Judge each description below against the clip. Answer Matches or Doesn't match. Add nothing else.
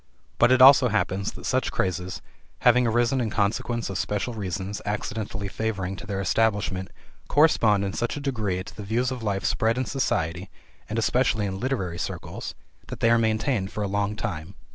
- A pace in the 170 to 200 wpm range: Matches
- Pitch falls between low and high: Doesn't match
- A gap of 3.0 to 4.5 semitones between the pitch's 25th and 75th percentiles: Matches